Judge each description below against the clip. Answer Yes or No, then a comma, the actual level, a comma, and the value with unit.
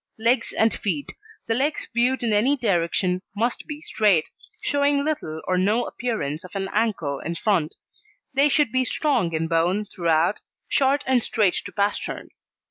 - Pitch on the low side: No, high, 215 Hz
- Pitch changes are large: Yes, wide, 6.4 semitones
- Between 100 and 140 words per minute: No, average, 160 wpm